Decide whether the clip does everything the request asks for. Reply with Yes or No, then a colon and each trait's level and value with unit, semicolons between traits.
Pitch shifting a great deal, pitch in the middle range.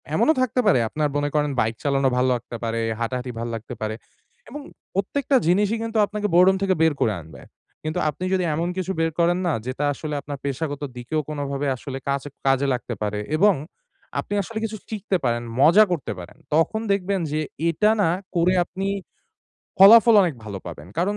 Yes: wide, 7.0 semitones; medium, 155 Hz